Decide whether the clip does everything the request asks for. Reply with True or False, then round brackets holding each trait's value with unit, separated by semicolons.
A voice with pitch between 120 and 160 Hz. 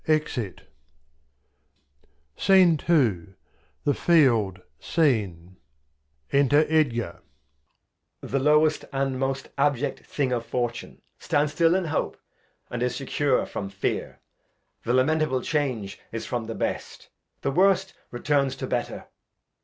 True (135 Hz)